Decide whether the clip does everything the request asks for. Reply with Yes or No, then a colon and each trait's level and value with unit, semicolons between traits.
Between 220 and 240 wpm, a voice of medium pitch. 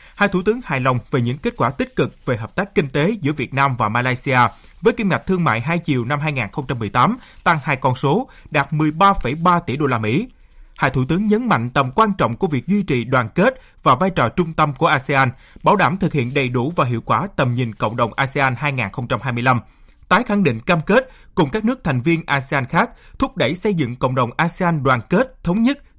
Yes: average, 230 wpm; medium, 145 Hz